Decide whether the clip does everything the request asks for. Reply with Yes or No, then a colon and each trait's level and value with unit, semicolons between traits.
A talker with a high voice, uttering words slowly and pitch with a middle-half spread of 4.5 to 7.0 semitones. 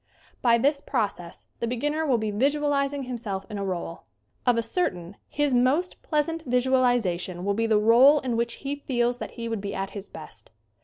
No: high, 240 Hz; average, 195 wpm; average, 5.1 semitones